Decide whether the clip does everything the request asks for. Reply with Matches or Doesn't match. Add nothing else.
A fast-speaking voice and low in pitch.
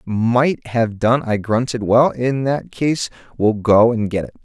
Doesn't match